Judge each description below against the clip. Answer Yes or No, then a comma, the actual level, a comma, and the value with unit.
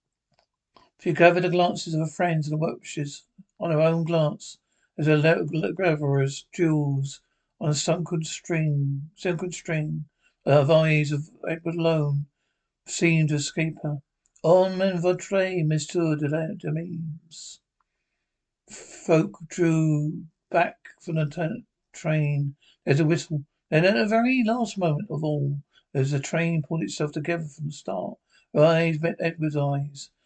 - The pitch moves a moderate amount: No, narrow, 2.2 semitones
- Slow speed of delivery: No, average, 145 wpm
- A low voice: No, medium, 160 Hz